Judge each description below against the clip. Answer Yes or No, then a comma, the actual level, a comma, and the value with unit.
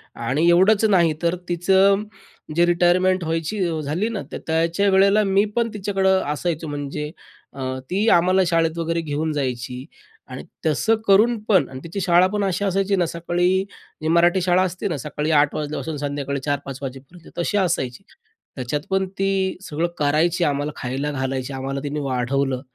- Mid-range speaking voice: Yes, medium, 170 Hz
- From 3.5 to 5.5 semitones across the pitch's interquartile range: Yes, average, 4.7 semitones